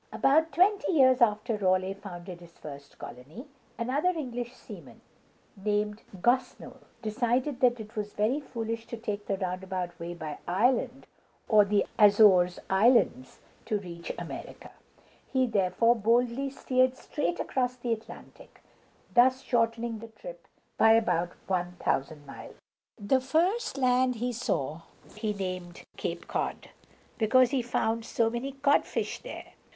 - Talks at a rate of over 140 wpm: No, slow, 135 wpm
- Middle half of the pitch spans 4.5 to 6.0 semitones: Yes, average, 4.9 semitones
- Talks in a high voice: Yes, high, 225 Hz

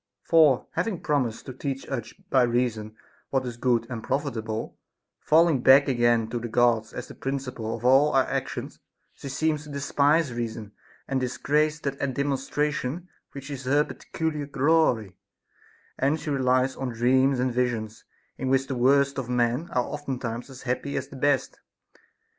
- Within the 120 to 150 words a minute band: No, average, 165 wpm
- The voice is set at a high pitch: No, low, 130 Hz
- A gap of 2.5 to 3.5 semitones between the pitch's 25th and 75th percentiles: Yes, average, 2.8 semitones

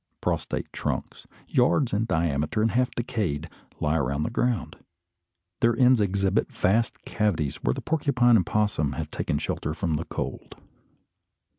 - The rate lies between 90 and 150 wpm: Yes, average, 145 wpm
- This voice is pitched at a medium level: No, low, 105 Hz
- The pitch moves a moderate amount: No, wide, 7.2 semitones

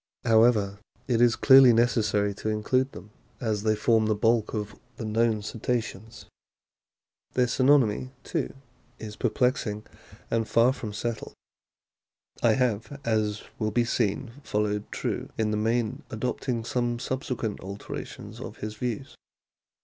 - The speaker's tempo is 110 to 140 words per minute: Yes, slow, 135 wpm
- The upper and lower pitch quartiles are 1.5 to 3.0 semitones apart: Yes, narrow, 2.4 semitones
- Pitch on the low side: Yes, low, 115 Hz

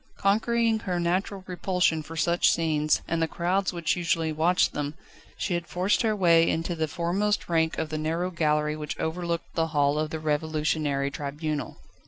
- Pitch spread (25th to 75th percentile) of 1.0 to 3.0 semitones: Yes, narrow, 2.6 semitones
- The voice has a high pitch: No, medium, 165 Hz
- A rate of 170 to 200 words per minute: Yes, average, 175 wpm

